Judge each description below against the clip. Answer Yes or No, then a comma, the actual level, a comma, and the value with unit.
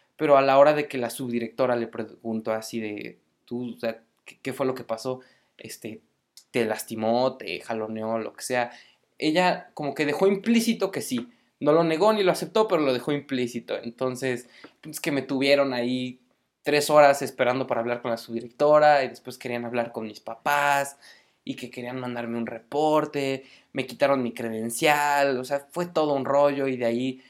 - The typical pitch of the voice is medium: No, low, 130 Hz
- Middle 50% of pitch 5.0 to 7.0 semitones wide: No, average, 3.7 semitones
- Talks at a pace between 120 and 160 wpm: No, fast, 190 wpm